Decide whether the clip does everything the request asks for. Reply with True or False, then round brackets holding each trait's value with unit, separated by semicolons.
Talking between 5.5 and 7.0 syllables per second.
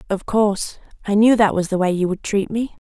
True (5.6 syllables/s)